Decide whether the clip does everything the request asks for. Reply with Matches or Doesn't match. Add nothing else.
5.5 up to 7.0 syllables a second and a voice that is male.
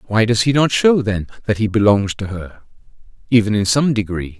Matches